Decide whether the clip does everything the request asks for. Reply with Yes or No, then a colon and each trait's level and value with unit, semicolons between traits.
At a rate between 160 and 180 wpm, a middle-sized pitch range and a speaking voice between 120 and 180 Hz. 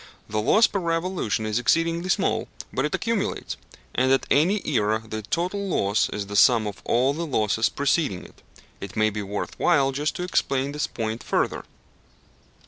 No: average, 175 wpm; wide, 7.6 semitones; low, 135 Hz